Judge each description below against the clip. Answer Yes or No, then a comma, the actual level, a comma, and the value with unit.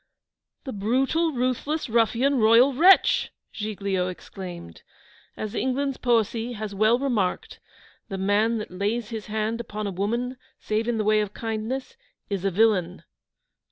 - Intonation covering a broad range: No, average, 3.4 semitones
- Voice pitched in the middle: No, high, 220 Hz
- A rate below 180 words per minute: Yes, average, 140 wpm